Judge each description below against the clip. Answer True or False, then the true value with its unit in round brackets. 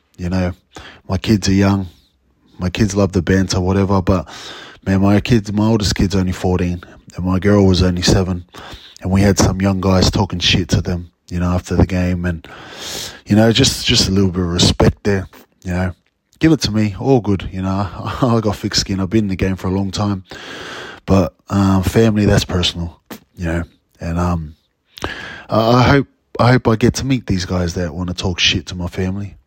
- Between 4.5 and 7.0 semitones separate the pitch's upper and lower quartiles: False (2.4 semitones)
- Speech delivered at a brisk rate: True (210 wpm)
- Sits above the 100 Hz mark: False (95 Hz)